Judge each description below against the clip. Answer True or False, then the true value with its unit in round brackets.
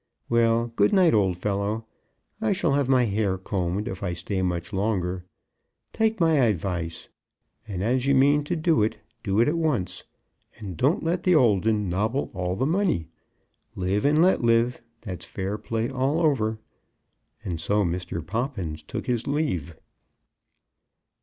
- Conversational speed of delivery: True (160 wpm)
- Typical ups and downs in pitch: False (6.9 semitones)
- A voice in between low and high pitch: False (110 Hz)